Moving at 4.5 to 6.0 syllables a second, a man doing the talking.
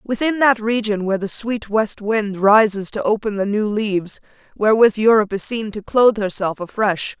No: 5.2 syllables/s; female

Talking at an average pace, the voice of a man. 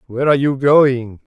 Yes: average, 180 wpm; male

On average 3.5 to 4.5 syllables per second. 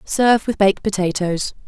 No: 5.4 syllables/s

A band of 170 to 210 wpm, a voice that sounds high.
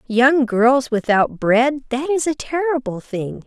No: average, 140 wpm; very high, 255 Hz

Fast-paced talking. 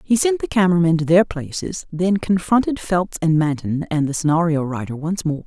Yes: fast, 210 wpm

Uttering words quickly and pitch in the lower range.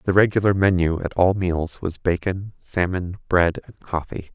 No: average, 165 wpm; very low, 90 Hz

